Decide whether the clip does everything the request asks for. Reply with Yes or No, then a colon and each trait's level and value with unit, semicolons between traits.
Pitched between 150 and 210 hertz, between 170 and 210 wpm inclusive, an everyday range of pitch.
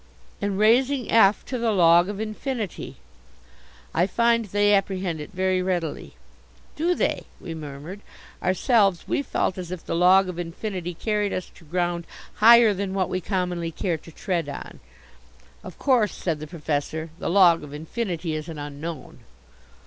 No: medium, 185 Hz; average, 160 wpm; average, 3.9 semitones